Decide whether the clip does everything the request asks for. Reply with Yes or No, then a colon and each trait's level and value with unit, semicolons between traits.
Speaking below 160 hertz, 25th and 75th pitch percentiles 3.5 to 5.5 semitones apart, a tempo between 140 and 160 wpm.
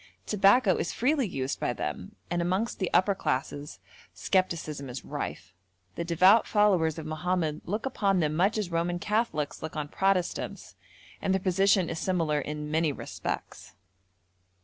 No: medium, 175 Hz; average, 4.2 semitones; average, 150 wpm